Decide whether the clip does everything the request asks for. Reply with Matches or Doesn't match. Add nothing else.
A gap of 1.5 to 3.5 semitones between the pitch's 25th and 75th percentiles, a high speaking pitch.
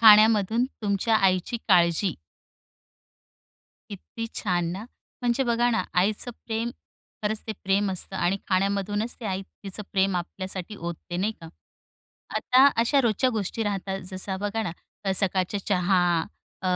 Matches